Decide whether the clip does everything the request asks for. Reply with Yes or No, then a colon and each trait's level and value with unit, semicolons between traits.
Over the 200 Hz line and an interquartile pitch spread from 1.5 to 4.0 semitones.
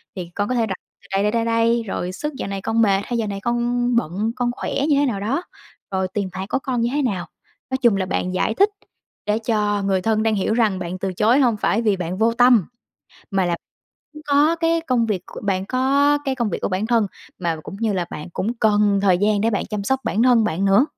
Yes: high, 220 Hz; average, 3.7 semitones